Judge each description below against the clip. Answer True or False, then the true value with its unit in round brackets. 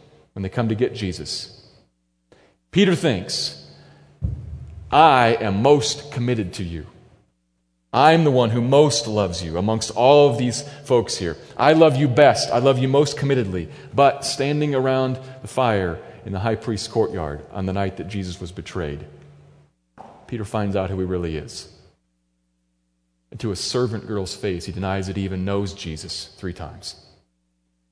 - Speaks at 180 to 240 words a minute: False (160 wpm)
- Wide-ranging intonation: True (7.2 semitones)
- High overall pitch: False (100 Hz)